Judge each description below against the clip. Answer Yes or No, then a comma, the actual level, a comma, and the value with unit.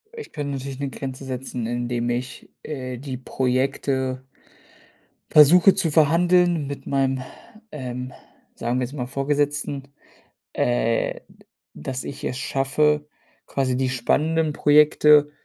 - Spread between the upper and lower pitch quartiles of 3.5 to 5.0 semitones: No, narrow, 2.6 semitones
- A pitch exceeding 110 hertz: Yes, low, 135 Hz